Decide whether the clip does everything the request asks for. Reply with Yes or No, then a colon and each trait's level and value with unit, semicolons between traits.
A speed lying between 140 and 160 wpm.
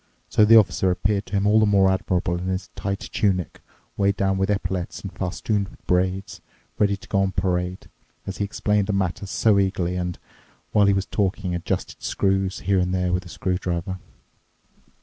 No: average, 190 wpm